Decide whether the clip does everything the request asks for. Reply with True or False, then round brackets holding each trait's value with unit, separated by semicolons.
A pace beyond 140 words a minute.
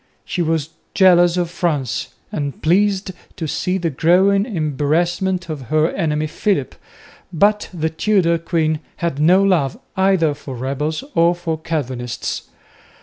False (135 wpm)